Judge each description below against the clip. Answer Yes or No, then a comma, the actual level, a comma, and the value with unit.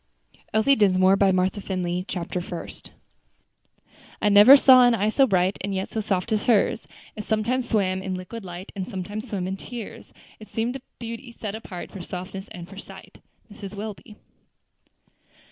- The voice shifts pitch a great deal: No, average, 3.2 semitones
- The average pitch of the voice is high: Yes, high, 200 Hz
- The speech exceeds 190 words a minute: No, average, 170 wpm